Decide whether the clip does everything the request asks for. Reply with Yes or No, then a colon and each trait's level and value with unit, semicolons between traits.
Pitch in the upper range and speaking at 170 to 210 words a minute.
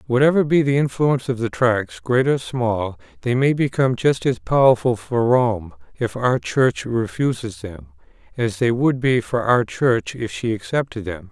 No: low, 125 Hz; average, 180 wpm